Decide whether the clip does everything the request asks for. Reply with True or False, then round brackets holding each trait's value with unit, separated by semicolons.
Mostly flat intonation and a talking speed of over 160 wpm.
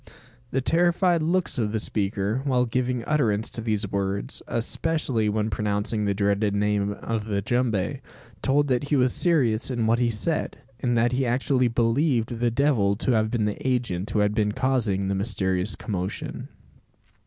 False (3.7 semitones; 170 wpm)